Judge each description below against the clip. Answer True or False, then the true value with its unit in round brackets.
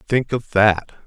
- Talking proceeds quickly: False (170 wpm)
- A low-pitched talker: True (110 Hz)